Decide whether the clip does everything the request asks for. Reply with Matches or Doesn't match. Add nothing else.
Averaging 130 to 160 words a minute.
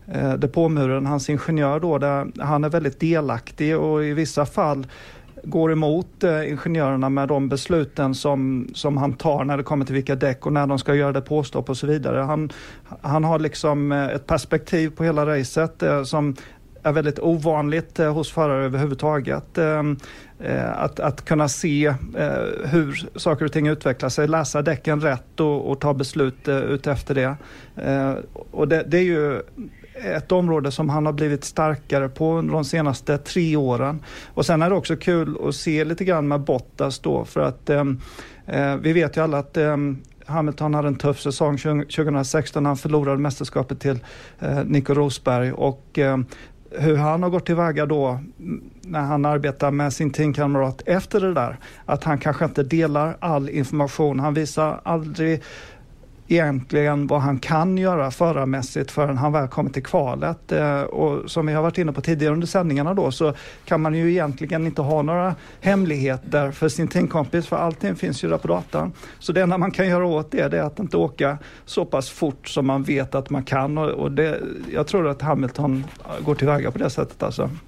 Doesn't match